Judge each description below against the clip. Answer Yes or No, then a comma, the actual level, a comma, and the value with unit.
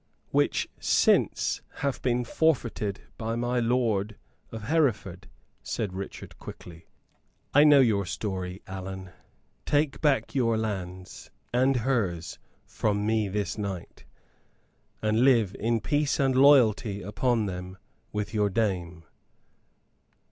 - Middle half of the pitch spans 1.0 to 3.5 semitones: No, average, 4.4 semitones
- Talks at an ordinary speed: No, slow, 115 wpm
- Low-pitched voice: Yes, low, 110 Hz